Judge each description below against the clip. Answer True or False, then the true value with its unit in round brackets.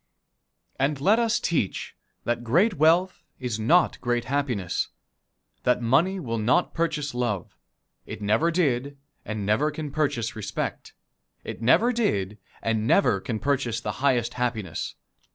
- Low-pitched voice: True (125 Hz)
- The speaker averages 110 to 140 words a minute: True (135 wpm)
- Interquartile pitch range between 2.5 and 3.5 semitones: False (5.4 semitones)